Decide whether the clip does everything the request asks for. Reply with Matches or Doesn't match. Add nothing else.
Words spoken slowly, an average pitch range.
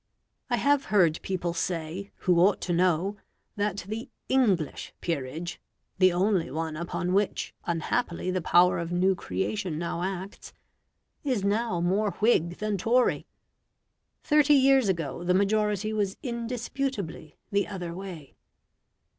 Matches